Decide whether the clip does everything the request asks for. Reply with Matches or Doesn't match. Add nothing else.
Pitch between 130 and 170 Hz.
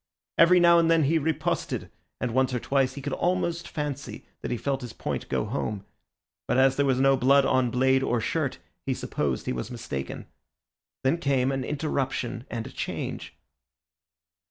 Matches